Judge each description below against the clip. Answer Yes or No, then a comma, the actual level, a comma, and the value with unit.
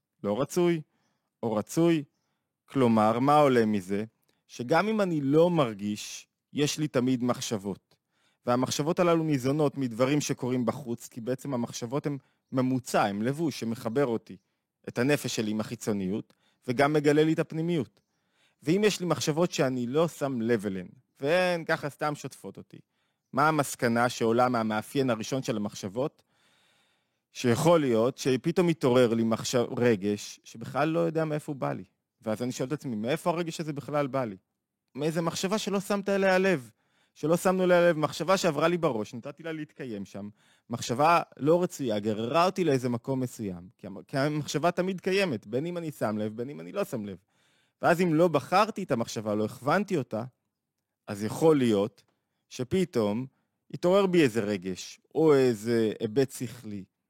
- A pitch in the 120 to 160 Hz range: Yes, medium, 140 Hz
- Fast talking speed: Yes, fast, 160 wpm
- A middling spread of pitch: No, wide, 5.9 semitones